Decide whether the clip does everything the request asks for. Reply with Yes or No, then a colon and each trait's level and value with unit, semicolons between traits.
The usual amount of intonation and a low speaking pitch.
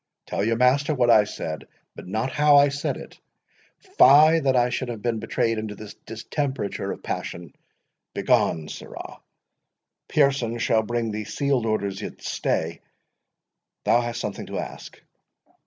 Yes: average, 4.3 semitones; low, 120 Hz